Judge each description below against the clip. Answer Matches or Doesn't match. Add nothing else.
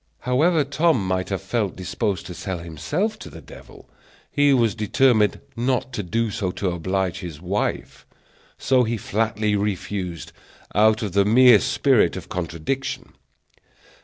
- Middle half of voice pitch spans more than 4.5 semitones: Matches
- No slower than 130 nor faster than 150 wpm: Matches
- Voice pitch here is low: Matches